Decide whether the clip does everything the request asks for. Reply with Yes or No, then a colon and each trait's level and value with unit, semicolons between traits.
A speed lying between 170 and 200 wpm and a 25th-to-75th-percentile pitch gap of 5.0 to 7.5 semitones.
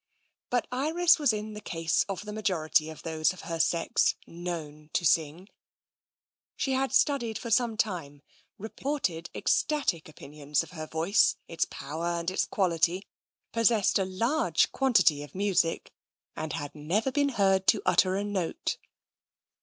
No: average, 150 wpm; wide, 5.6 semitones